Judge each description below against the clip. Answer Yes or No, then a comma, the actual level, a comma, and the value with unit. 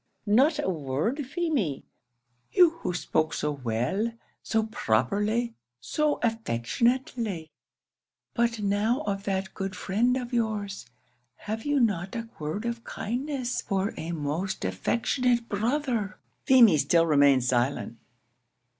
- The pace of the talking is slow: Yes, slow, 120 wpm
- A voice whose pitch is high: Yes, high, 210 Hz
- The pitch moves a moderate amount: No, wide, 7.1 semitones